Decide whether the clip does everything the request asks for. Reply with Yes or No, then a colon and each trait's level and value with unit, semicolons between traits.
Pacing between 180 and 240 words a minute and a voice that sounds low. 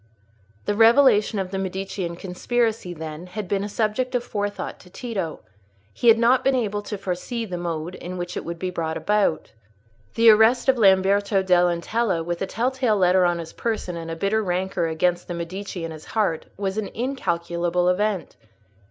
No: average, 190 wpm; high, 190 Hz